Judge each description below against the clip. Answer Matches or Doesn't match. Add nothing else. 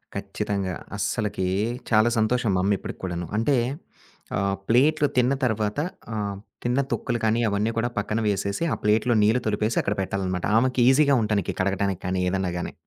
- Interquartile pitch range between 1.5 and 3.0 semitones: Doesn't match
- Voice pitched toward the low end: Matches